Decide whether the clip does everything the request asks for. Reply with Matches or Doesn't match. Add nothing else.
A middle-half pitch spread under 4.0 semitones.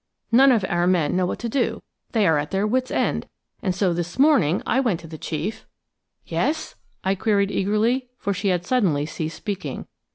Doesn't match